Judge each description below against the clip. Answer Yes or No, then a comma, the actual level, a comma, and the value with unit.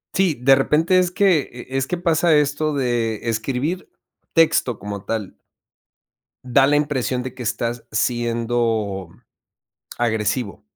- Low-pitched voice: Yes, low, 125 Hz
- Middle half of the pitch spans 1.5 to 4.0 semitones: No, average, 4.6 semitones